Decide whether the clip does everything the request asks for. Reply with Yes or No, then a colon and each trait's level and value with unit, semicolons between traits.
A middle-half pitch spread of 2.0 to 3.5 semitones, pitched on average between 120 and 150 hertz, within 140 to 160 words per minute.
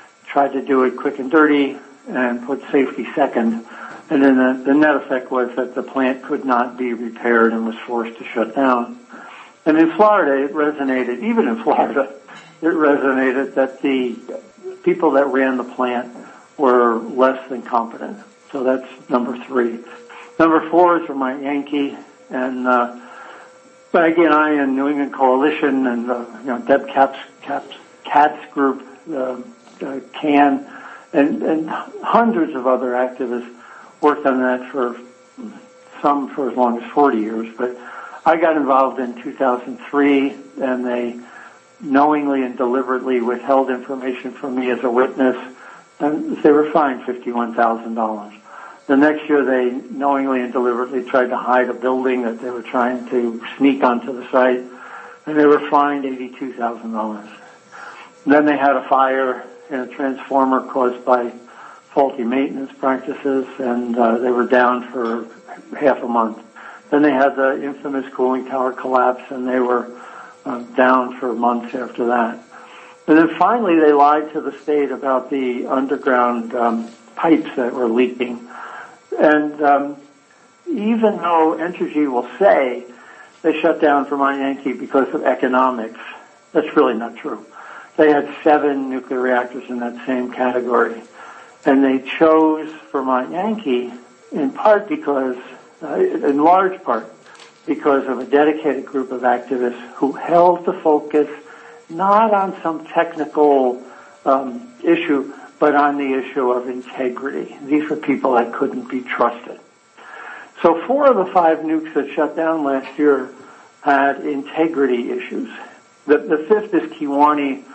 Yes: average, 3.0 semitones; low, 135 Hz; average, 155 wpm